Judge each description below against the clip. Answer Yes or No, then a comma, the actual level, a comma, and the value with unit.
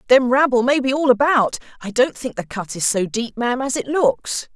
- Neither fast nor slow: No, fast, 235 wpm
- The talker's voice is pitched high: Yes, high, 245 Hz